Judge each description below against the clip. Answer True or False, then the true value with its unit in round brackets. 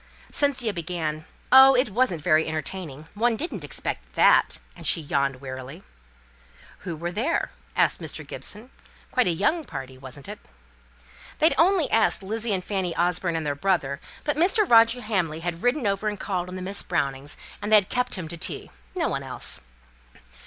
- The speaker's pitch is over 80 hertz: True (185 Hz)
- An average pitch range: False (6.7 semitones)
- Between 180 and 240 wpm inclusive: False (170 wpm)